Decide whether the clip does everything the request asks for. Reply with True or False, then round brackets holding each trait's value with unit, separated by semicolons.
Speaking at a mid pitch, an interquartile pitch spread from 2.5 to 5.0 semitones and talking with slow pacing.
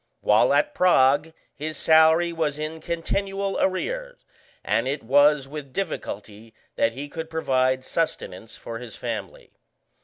True (155 Hz; 4.4 semitones; 130 wpm)